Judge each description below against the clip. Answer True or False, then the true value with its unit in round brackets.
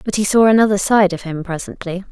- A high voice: True (195 Hz)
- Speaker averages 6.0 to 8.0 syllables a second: True (6.1 syllables/s)